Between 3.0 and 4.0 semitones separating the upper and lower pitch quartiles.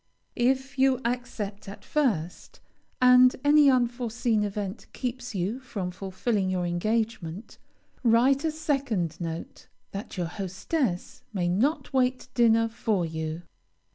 No: average, 5.3 semitones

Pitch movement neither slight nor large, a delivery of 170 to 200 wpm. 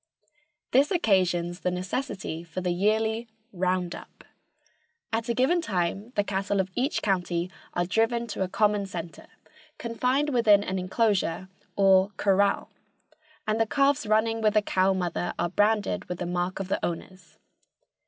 No: average, 3.6 semitones; average, 155 wpm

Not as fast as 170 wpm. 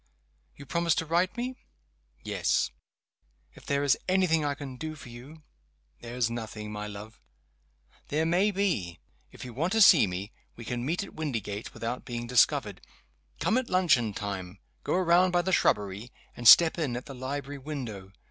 No: average, 185 wpm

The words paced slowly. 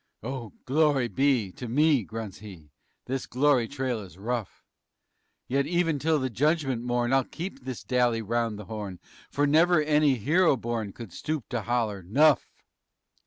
No: average, 160 wpm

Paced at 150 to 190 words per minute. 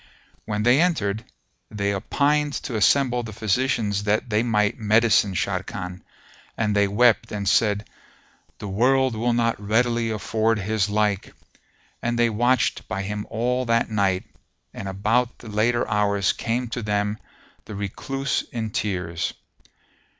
No: average, 140 wpm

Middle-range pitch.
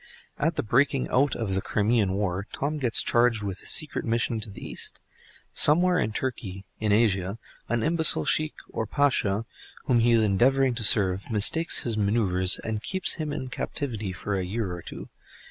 No: low, 115 Hz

